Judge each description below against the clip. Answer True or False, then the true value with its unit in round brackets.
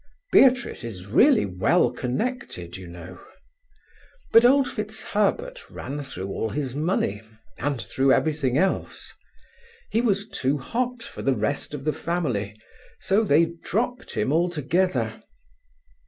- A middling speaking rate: False (125 wpm)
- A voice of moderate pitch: True (150 Hz)